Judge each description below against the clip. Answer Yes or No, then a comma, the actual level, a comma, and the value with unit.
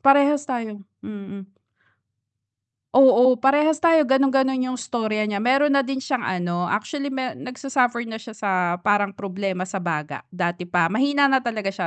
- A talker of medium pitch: No, high, 240 Hz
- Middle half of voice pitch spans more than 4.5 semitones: Yes, average, 5.2 semitones